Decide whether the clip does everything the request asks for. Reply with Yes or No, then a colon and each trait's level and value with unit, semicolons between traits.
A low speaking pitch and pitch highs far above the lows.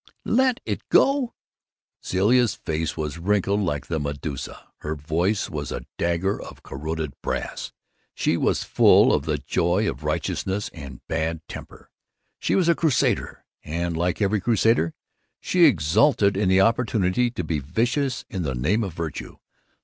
Yes: very low, 90 Hz; wide, 6.0 semitones